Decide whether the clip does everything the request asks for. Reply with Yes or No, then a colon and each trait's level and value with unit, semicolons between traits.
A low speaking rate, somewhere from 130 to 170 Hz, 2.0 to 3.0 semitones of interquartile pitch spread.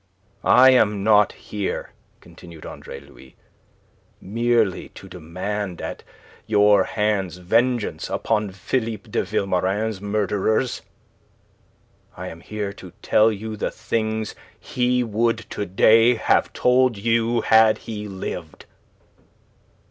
No: slow, 110 wpm; low, 105 Hz; narrow, 2.6 semitones